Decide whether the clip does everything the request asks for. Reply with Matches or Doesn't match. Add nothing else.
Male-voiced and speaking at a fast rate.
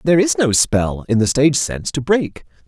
Matches